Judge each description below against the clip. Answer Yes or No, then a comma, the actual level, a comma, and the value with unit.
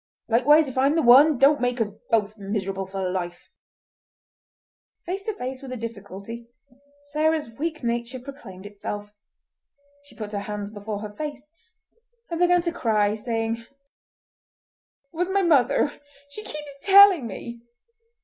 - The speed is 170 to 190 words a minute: No, average, 140 wpm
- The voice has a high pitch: Yes, high, 240 Hz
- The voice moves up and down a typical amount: No, wide, 6.3 semitones